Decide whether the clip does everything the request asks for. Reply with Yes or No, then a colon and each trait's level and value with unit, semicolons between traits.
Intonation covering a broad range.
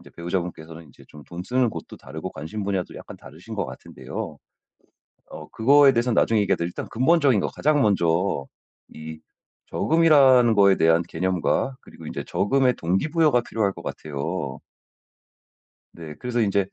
Yes: wide, 7.0 semitones